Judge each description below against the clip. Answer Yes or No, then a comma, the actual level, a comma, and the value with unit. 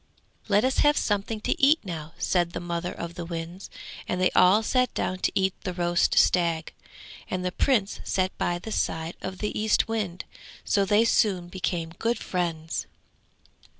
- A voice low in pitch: No, medium, 185 Hz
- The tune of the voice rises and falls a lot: No, average, 3.4 semitones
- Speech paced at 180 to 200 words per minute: No, average, 170 wpm